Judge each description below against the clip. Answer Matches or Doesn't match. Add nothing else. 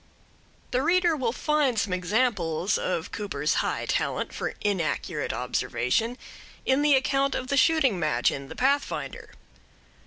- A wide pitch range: Matches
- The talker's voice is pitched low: Doesn't match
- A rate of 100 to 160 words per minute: Matches